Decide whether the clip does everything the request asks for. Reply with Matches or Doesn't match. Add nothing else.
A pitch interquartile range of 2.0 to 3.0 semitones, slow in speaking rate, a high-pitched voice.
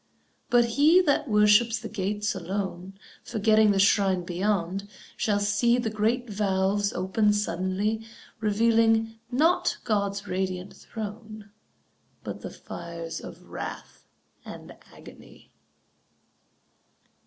Matches